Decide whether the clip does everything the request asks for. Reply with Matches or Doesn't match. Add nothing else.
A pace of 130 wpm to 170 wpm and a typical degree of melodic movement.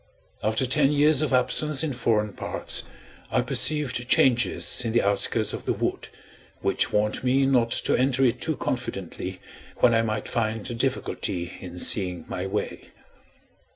Matches